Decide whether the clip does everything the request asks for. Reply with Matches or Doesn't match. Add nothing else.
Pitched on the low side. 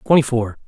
Matches